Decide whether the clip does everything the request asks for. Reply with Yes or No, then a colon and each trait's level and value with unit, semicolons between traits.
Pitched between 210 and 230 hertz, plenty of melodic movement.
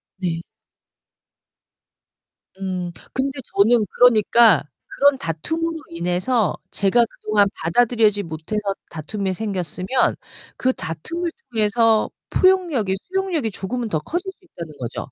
Yes: high, 215 Hz; wide, 6.2 semitones